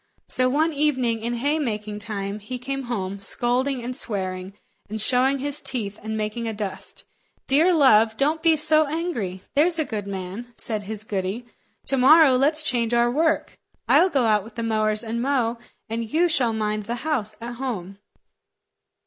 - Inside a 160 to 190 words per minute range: Yes, average, 175 wpm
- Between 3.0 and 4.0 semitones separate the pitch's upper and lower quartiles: No, average, 4.6 semitones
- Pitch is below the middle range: No, high, 235 Hz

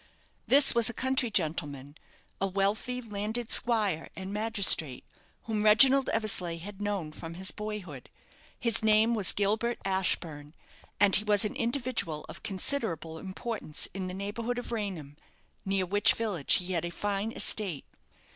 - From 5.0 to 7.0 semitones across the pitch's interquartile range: No, average, 4.1 semitones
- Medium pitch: No, high, 205 Hz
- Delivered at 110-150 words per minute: Yes, average, 145 wpm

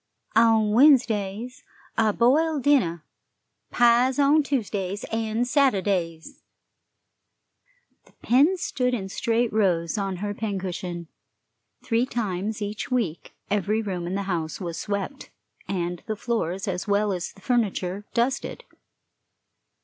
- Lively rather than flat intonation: No, average, 4.2 semitones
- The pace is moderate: No, slow, 120 wpm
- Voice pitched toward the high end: Yes, high, 210 Hz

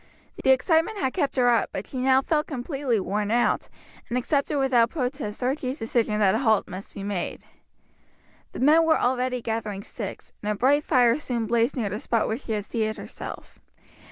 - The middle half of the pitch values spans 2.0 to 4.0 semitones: Yes, average, 3.7 semitones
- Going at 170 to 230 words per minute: Yes, average, 190 wpm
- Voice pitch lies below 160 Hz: No, high, 245 Hz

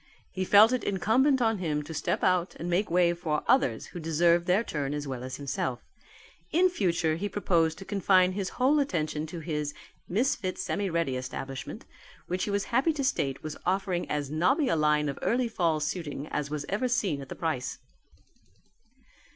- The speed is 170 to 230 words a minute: Yes, average, 185 wpm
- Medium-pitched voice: Yes, medium, 175 Hz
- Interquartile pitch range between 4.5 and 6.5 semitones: Yes, average, 5.2 semitones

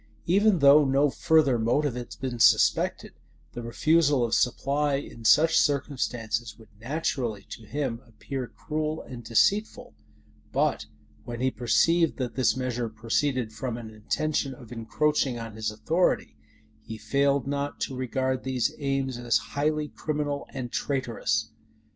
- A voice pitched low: Yes, low, 130 Hz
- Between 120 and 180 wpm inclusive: Yes, average, 140 wpm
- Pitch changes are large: No, average, 3.7 semitones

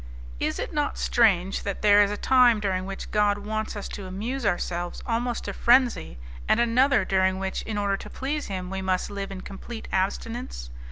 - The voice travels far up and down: No, average, 3.4 semitones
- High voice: Yes, high, 205 Hz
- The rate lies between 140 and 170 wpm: No, average, 190 wpm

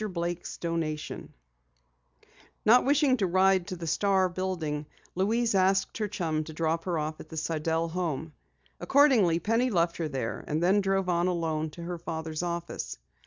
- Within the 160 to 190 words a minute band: Yes, average, 165 wpm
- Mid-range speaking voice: Yes, medium, 175 Hz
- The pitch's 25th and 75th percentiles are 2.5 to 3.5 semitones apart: Yes, average, 3.1 semitones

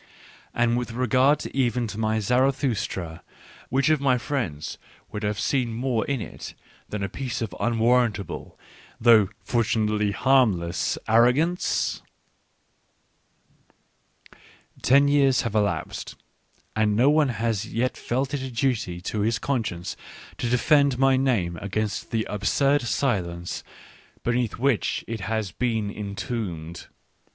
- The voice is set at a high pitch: No, low, 115 Hz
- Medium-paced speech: No, slow, 125 wpm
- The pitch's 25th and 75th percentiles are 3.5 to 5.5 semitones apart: Yes, average, 3.8 semitones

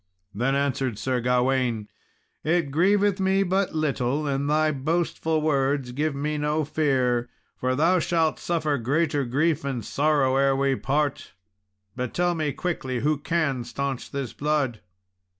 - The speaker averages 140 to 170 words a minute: Yes, average, 145 wpm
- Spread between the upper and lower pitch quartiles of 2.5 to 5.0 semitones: Yes, average, 3.1 semitones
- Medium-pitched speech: Yes, medium, 145 Hz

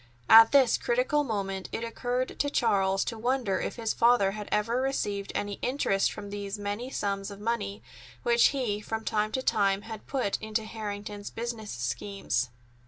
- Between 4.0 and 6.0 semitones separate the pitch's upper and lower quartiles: No, average, 3.0 semitones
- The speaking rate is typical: Yes, average, 170 wpm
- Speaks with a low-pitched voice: No, high, 215 Hz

